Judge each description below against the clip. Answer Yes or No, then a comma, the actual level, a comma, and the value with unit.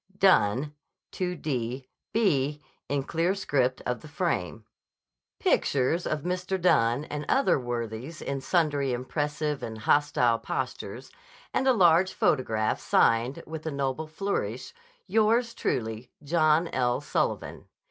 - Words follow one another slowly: Yes, slow, 120 wpm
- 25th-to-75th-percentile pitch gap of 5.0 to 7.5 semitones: Yes, wide, 5.4 semitones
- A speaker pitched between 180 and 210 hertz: No, medium, 145 Hz